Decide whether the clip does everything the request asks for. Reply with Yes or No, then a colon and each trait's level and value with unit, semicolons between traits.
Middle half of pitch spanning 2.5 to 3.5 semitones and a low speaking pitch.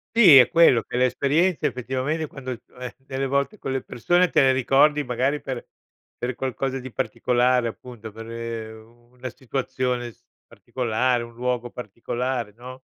No: narrow, 2.0 semitones; low, 125 Hz